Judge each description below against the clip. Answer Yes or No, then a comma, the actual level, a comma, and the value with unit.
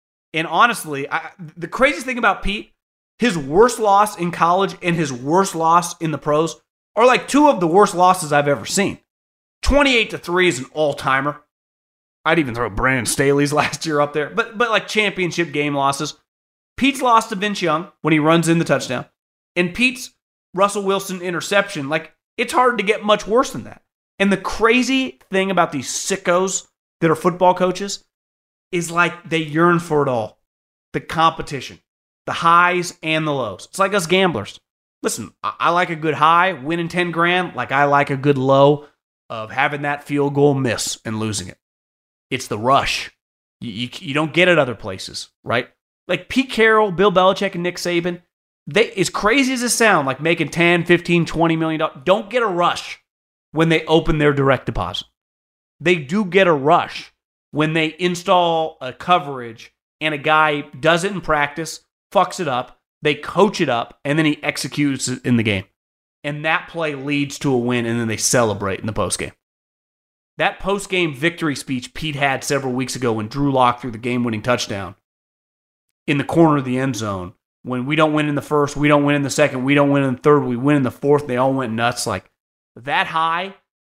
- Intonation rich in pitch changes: No, average, 4.6 semitones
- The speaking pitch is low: No, medium, 155 Hz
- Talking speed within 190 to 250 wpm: Yes, average, 195 wpm